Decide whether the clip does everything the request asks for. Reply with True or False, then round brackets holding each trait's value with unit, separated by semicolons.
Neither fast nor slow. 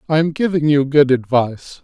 True (195 wpm)